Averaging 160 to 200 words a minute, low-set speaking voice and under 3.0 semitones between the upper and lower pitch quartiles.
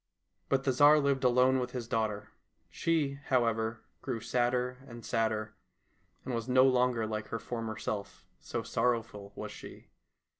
No: average, 150 wpm; low, 120 Hz; narrow, 2.4 semitones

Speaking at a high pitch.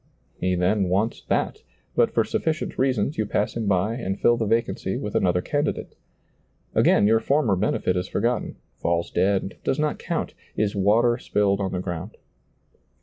No: low, 105 Hz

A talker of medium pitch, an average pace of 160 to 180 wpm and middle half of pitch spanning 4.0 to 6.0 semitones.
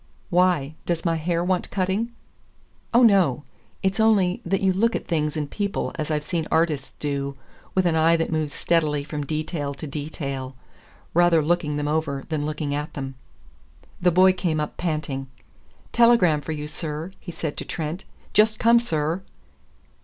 No: medium, 160 Hz; average, 170 wpm; average, 3.5 semitones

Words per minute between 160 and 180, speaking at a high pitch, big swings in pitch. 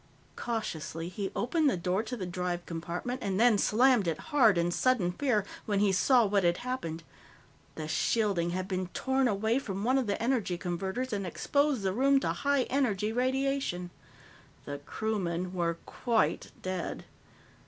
Yes: average, 165 wpm; high, 205 Hz; wide, 6.0 semitones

